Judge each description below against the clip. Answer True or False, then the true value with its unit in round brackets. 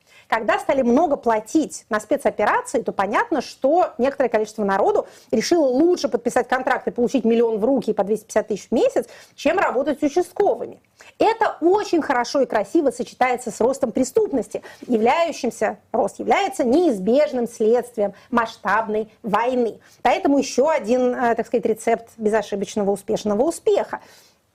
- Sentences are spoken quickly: False (135 wpm)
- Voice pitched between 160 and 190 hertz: False (245 Hz)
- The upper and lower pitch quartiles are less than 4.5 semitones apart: False (5.2 semitones)